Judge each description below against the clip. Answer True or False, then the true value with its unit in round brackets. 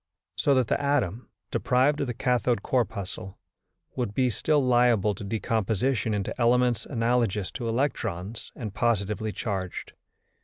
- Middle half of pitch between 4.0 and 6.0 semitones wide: False (3.4 semitones)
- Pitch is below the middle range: True (115 Hz)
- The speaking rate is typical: False (130 wpm)